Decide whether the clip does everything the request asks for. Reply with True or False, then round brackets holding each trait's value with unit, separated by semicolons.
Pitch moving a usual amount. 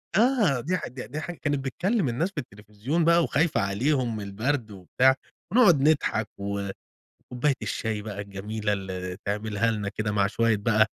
False (6.4 semitones)